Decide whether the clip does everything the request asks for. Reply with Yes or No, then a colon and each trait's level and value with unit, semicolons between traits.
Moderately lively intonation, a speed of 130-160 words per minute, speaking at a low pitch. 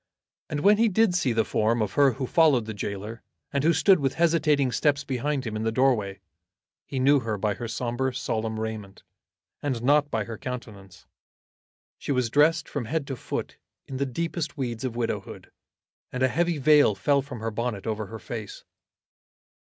No: average, 4.6 semitones; average, 185 wpm; low, 125 Hz